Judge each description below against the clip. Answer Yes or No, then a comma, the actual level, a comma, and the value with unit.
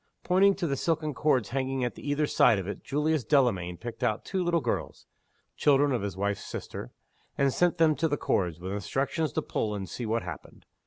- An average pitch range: No, wide, 6.6 semitones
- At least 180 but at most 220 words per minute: Yes, fast, 205 wpm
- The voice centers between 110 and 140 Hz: Yes, low, 135 Hz